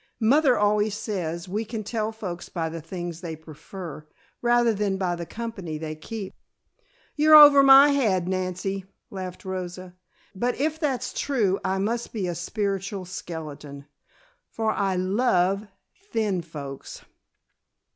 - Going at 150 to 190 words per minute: No, slow, 135 wpm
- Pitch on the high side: Yes, high, 195 Hz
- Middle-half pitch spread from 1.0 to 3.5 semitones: No, average, 4.3 semitones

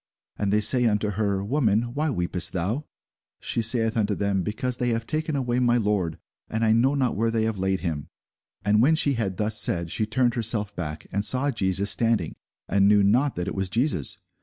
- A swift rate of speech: Yes, fast, 210 wpm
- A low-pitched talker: Yes, low, 110 Hz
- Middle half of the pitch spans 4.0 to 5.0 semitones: No, average, 3.5 semitones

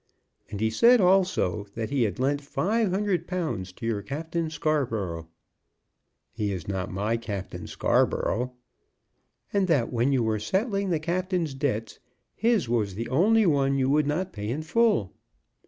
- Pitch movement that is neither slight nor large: No, wide, 8.7 semitones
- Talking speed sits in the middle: Yes, average, 155 wpm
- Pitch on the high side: No, medium, 140 Hz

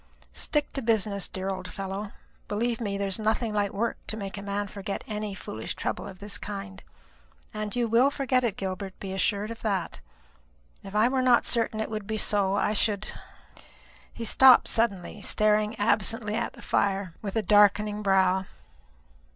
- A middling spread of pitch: No, narrow, 2.1 semitones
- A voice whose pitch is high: Yes, high, 210 Hz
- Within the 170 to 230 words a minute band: Yes, average, 180 wpm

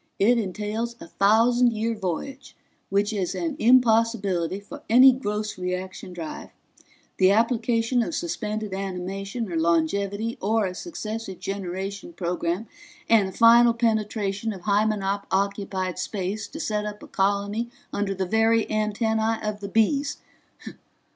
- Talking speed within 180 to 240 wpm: No, slow, 135 wpm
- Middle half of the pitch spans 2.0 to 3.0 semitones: Yes, average, 2.7 semitones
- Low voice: No, high, 210 Hz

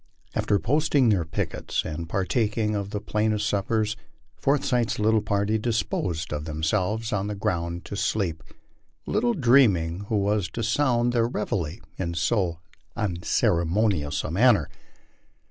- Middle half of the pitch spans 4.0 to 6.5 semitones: Yes, average, 4.8 semitones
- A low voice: Yes, low, 105 Hz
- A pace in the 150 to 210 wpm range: No, average, 140 wpm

